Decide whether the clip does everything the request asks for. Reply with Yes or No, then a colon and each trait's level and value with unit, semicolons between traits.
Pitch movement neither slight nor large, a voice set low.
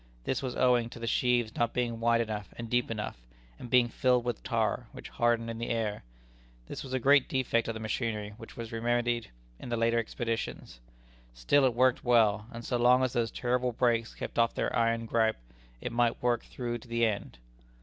No: narrow, 1.3 semitones; low, 115 Hz